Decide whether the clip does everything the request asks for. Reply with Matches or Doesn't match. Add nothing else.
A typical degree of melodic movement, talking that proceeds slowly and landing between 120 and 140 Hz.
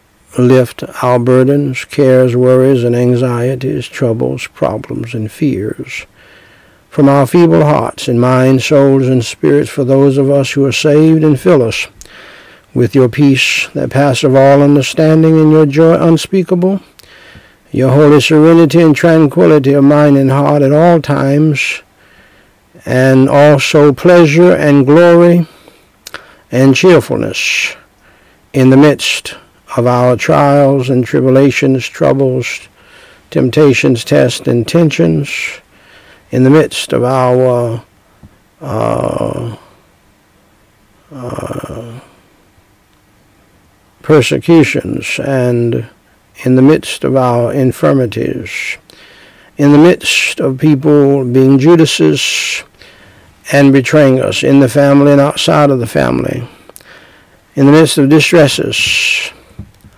Matches